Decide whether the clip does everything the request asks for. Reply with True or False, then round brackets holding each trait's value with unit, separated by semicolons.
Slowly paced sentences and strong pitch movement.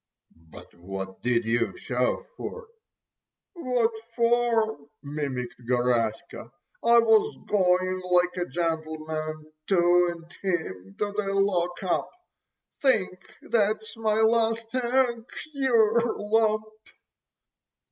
True (90 wpm; 6.3 semitones)